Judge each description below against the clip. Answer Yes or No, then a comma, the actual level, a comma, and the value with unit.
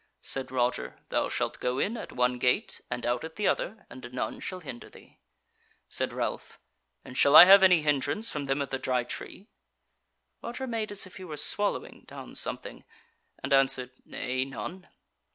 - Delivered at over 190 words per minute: No, average, 180 wpm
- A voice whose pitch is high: No, medium, 140 Hz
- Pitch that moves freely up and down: Yes, wide, 6.8 semitones